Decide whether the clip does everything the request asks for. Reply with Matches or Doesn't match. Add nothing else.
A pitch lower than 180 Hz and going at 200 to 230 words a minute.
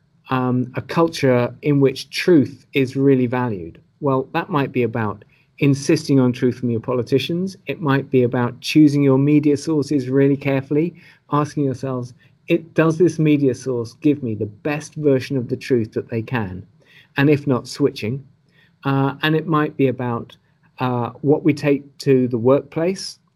Doesn't match